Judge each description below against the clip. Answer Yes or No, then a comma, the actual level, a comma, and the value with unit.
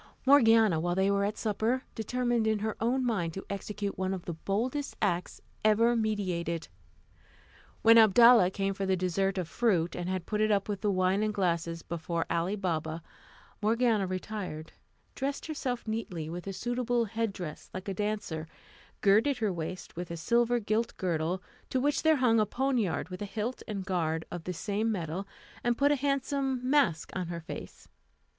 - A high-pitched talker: Yes, high, 205 Hz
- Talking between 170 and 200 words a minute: Yes, average, 180 wpm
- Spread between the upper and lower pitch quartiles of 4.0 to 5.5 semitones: Yes, average, 4.4 semitones